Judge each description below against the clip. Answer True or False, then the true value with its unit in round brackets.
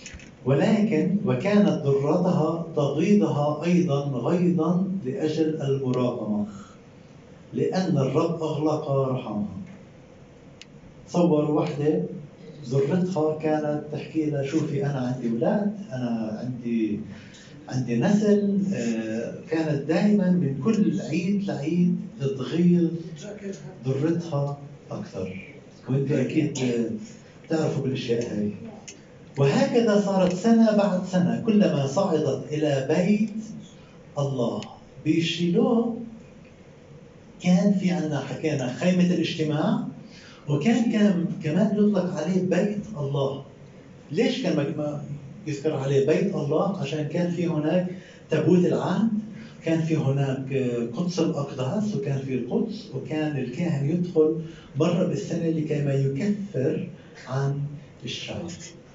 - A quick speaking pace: False (95 wpm)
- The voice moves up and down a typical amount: True (4.4 semitones)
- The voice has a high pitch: False (160 Hz)